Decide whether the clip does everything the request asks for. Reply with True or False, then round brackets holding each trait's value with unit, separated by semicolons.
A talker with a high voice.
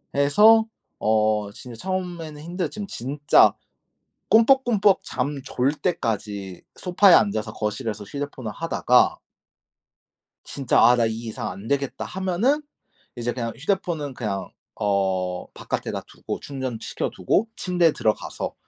False (135 Hz)